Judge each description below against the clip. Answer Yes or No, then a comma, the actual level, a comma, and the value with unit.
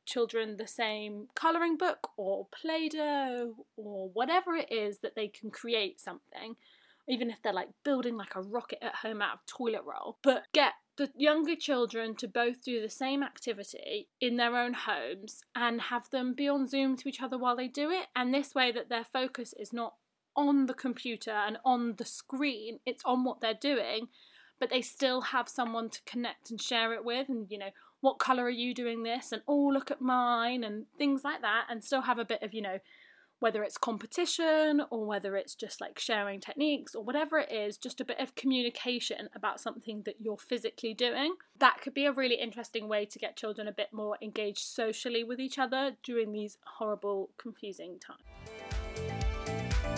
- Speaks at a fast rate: No, average, 195 wpm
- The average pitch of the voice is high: Yes, high, 240 Hz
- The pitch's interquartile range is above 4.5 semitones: No, average, 3.3 semitones